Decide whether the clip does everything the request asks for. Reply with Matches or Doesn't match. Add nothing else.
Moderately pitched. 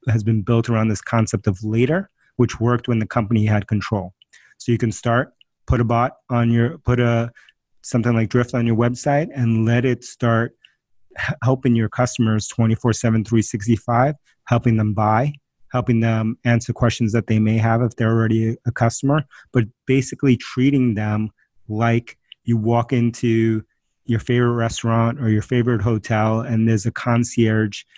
Doesn't match